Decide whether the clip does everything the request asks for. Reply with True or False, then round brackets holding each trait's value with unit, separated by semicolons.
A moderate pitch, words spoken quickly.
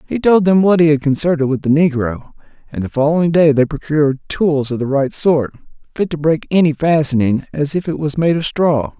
True (150 Hz; 220 wpm)